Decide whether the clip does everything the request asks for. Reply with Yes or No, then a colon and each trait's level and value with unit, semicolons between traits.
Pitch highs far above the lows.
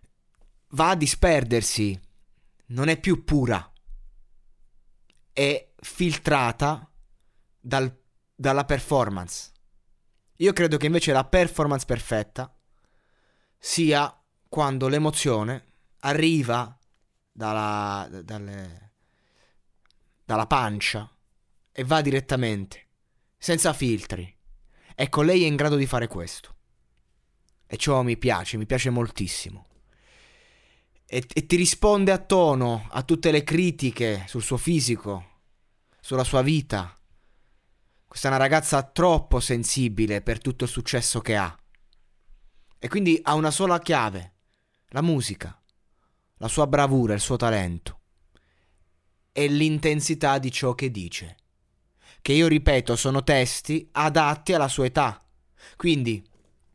Yes: wide, 6.4 semitones